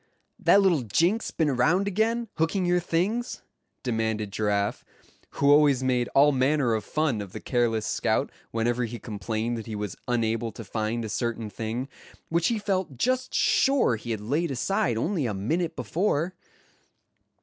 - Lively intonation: Yes, wide, 7.3 semitones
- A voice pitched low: Yes, low, 125 Hz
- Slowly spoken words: No, average, 160 wpm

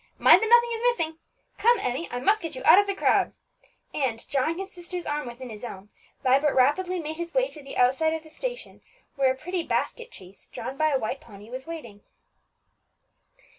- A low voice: No, very high, 310 Hz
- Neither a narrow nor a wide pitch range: No, wide, 6.2 semitones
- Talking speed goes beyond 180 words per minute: Yes, fast, 205 wpm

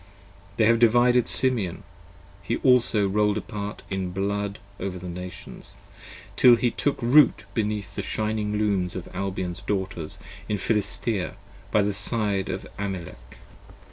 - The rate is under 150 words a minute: Yes, average, 140 wpm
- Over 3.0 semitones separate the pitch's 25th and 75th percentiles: No, average, 2.7 semitones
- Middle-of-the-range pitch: No, low, 105 Hz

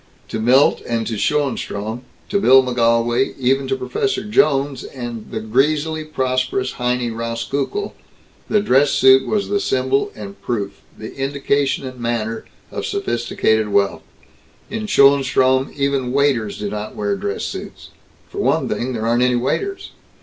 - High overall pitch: No, low, 130 Hz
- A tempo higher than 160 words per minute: No, average, 145 wpm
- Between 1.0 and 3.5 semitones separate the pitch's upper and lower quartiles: Yes, average, 3.2 semitones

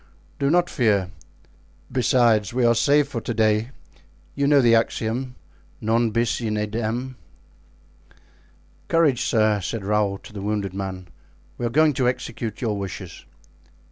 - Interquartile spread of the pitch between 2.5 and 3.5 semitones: Yes, average, 3.1 semitones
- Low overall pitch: Yes, low, 115 Hz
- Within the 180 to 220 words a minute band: No, average, 140 wpm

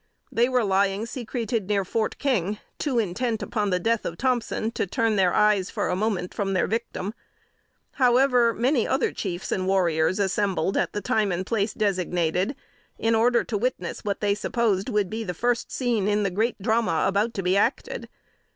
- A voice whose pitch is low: No, high, 210 Hz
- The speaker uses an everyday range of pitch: Yes, average, 3.5 semitones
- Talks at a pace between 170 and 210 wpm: Yes, average, 185 wpm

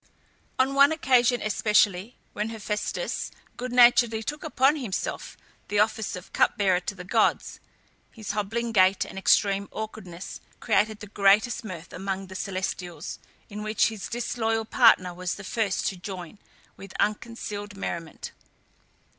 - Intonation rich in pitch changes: No, average, 3.2 semitones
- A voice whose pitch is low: No, high, 210 Hz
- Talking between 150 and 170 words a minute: No, average, 140 wpm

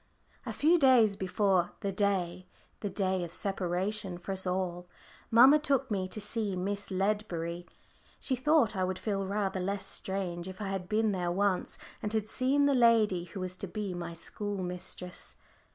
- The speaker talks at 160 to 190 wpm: Yes, average, 175 wpm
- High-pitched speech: Yes, high, 195 Hz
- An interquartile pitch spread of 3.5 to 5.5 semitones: No, average, 2.8 semitones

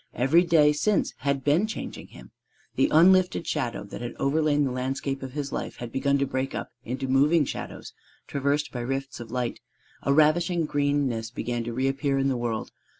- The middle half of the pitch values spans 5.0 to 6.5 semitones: No, average, 2.8 semitones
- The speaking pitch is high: No, medium, 140 Hz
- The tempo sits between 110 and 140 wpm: No, average, 185 wpm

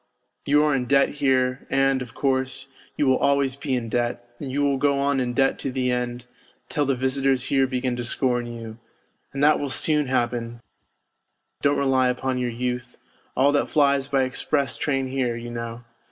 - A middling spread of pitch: No, narrow, 2.0 semitones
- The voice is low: Yes, low, 130 Hz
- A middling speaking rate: Yes, average, 190 wpm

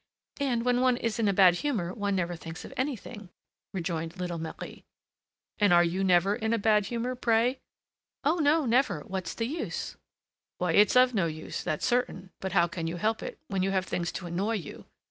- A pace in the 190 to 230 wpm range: Yes, fast, 205 wpm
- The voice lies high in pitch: Yes, high, 200 Hz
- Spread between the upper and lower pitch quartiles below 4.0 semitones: No, wide, 5.5 semitones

